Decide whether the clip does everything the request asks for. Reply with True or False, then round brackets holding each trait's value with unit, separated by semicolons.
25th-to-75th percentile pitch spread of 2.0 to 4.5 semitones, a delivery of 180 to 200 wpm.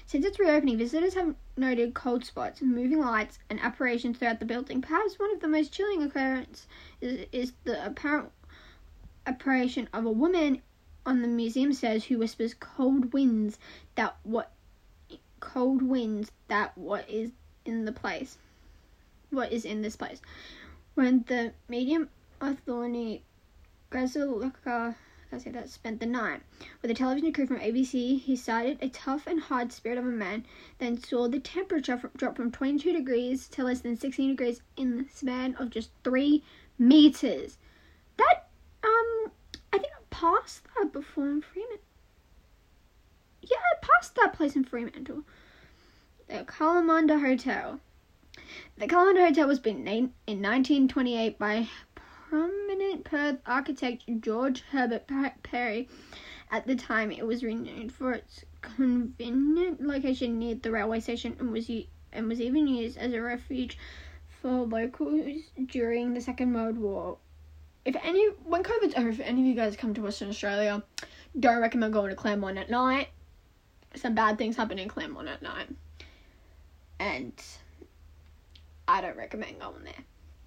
False (4.0 semitones; 150 wpm)